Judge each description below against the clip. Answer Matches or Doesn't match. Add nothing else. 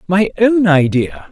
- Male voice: Matches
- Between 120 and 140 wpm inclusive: Matches